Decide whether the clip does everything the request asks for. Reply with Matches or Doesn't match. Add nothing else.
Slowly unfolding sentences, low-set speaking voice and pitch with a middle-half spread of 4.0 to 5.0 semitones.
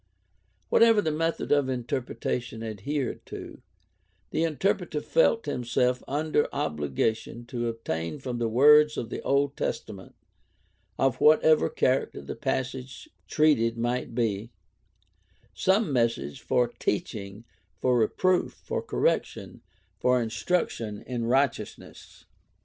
Matches